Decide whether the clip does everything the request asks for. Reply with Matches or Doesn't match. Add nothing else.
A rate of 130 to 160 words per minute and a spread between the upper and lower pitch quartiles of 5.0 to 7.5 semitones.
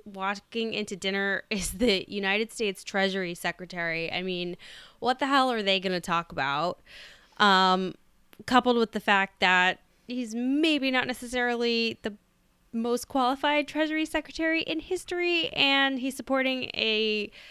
Matches